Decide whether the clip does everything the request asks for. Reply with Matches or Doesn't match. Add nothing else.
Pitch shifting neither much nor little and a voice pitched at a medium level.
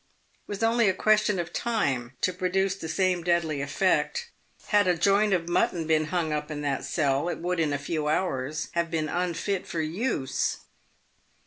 Matches